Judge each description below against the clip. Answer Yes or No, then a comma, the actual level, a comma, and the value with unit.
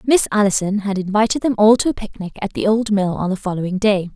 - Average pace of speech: No, fast, 245 wpm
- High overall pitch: Yes, high, 205 Hz